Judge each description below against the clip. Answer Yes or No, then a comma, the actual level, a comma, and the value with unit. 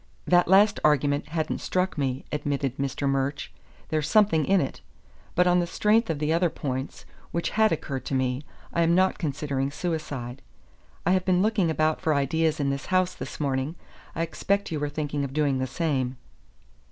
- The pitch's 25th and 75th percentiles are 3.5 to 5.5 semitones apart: Yes, average, 4.3 semitones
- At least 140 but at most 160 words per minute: No, average, 185 wpm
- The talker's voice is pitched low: No, medium, 155 Hz